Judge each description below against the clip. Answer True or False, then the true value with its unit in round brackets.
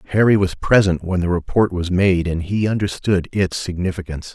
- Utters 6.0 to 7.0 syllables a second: False (5.5 syllables/s)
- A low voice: True (90 Hz)